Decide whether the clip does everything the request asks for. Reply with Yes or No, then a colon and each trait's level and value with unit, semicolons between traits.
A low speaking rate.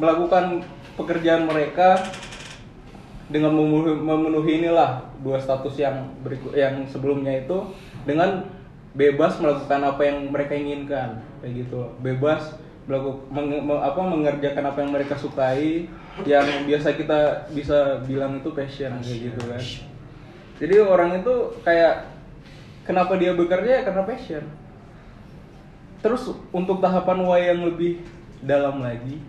No: average, 120 wpm